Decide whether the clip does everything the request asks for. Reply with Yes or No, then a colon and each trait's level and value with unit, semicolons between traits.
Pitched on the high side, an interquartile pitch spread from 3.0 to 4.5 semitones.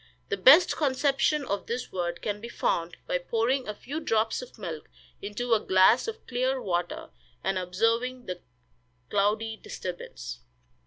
No: high, 225 Hz; wide, 5.4 semitones